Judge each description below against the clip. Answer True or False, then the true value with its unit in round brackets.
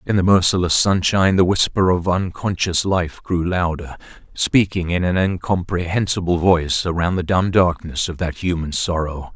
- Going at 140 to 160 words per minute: True (155 wpm)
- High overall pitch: False (90 Hz)